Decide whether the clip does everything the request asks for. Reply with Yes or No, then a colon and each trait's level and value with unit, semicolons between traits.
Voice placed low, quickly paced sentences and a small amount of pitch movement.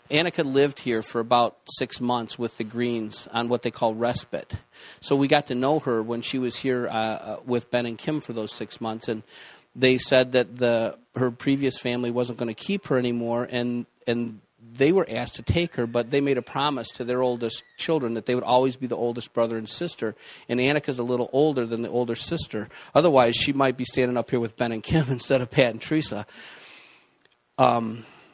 Yes: low, 120 Hz; fast, 220 wpm; narrow, 2.1 semitones